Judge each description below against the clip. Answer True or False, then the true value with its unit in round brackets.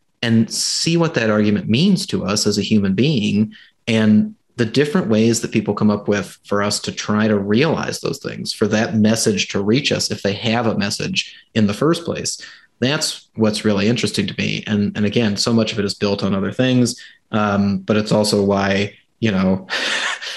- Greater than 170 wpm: True (205 wpm)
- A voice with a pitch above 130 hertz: False (110 Hz)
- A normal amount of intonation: True (3.1 semitones)